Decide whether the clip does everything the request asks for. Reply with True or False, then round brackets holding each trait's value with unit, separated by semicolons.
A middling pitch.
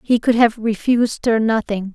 False (225 Hz)